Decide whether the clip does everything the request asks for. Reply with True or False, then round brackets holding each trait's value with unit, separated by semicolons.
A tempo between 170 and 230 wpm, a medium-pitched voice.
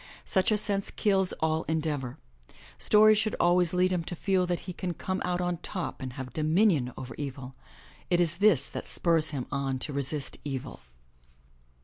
True (185 wpm; 170 Hz)